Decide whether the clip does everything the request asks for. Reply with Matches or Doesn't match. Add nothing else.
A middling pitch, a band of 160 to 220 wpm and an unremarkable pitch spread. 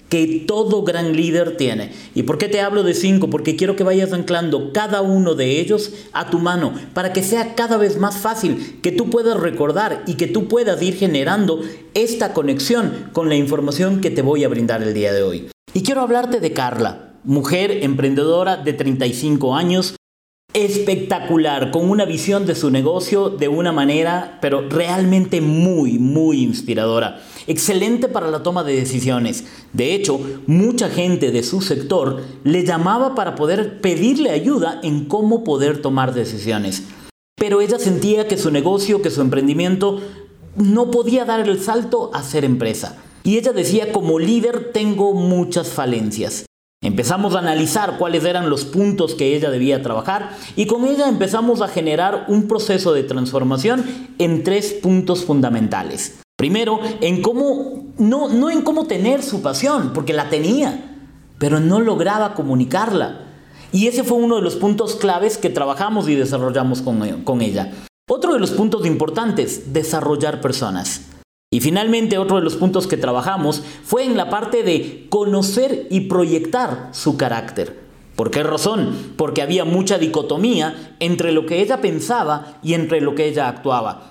Doesn't match